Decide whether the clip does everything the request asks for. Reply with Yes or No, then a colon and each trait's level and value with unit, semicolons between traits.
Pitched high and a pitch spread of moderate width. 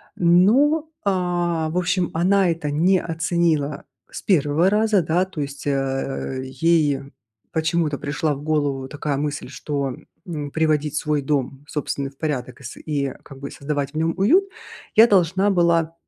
No: medium, 155 Hz; average, 3.7 semitones